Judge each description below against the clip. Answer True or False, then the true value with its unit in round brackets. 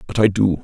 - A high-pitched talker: False (100 Hz)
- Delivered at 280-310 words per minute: True (285 wpm)